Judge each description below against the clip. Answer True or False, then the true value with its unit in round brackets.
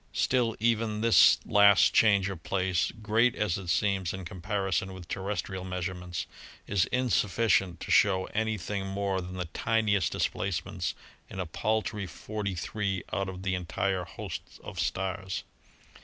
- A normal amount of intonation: False (2.3 semitones)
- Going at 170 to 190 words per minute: False (145 wpm)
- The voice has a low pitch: True (95 Hz)